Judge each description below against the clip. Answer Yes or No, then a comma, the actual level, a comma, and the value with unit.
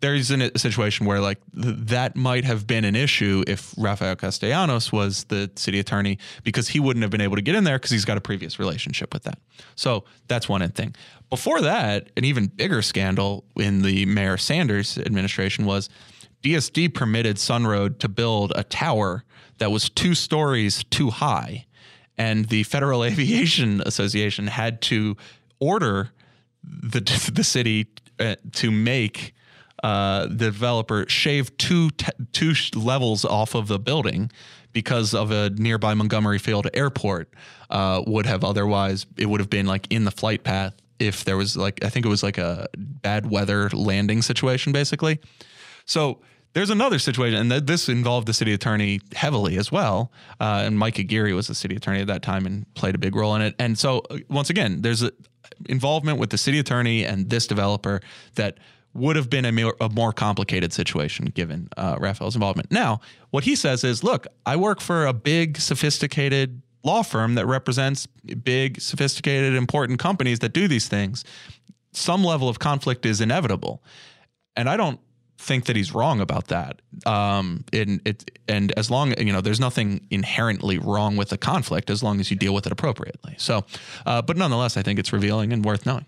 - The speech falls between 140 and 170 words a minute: No, average, 185 wpm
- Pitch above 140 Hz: No, low, 110 Hz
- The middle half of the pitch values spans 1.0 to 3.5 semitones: No, average, 4.3 semitones